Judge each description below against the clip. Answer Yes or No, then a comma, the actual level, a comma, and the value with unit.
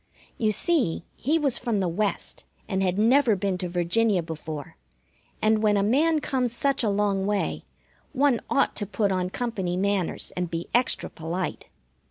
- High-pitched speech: Yes, high, 205 Hz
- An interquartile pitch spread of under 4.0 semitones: No, average, 4.9 semitones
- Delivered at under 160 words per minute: No, average, 170 wpm